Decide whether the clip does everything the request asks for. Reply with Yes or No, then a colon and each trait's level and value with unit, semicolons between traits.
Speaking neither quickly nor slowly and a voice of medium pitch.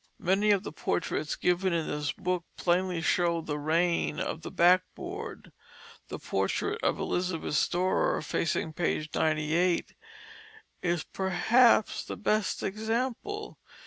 No: slow, 120 wpm; medium, 180 Hz